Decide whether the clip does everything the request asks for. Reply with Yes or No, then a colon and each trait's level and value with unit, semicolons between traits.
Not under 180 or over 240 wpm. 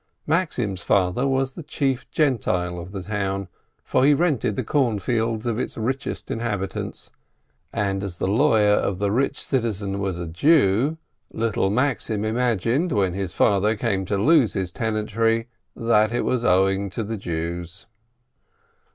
No: average, 150 wpm